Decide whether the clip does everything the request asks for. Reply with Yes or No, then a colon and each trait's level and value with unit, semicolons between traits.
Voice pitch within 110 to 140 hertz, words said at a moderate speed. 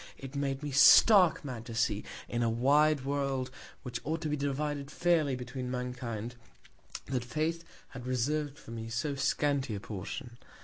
Yes: low, 135 Hz; average, 165 wpm